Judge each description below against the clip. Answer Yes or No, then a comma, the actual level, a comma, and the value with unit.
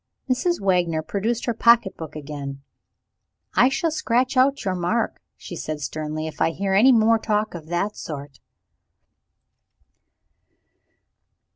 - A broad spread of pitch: Yes, wide, 7.0 semitones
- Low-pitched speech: No, high, 195 Hz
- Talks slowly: Yes, slow, 130 wpm